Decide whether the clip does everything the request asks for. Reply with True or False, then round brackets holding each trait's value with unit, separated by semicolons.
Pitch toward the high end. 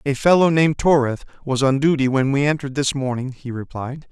False (140 Hz)